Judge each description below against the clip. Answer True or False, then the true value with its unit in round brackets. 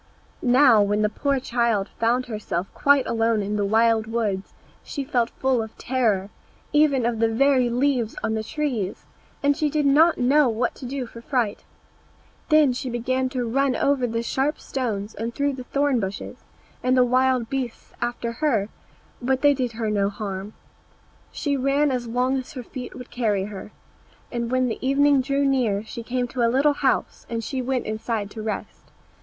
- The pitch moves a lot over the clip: False (3.3 semitones)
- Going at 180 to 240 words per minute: True (185 wpm)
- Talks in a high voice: True (245 Hz)